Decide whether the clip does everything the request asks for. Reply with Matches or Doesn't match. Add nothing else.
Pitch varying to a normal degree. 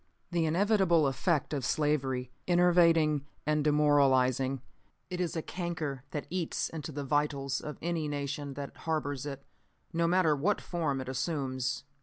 Matches